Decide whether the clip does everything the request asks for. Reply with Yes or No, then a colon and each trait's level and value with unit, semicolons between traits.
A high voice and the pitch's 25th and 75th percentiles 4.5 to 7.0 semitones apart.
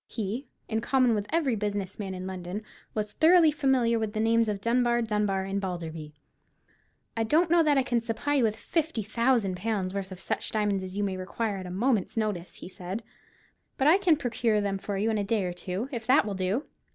No: high, 215 Hz; average, 4.1 semitones